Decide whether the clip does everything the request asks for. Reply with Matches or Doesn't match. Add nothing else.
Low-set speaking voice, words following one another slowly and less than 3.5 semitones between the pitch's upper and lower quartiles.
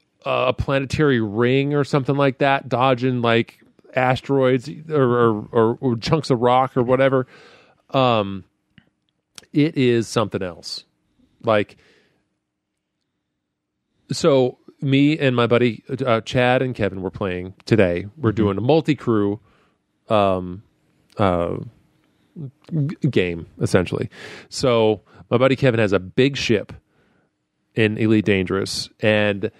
Doesn't match